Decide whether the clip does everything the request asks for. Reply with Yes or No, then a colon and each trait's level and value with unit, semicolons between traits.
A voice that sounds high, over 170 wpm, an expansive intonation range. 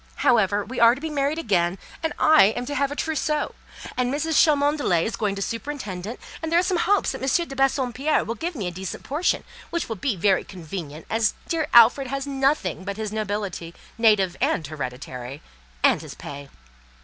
Yes: high, 235 Hz; average, 195 wpm; wide, 7.2 semitones